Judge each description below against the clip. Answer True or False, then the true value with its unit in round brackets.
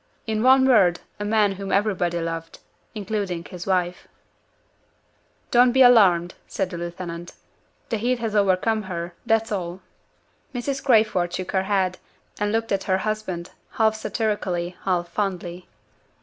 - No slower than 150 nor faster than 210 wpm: False (140 wpm)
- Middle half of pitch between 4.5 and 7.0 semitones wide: False (3.7 semitones)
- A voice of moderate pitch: False (195 Hz)